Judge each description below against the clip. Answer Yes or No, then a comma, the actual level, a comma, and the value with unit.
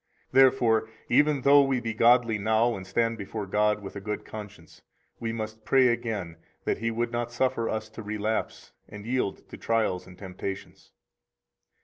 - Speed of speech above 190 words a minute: No, average, 165 wpm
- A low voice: Yes, low, 110 Hz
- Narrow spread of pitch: Yes, narrow, 2.3 semitones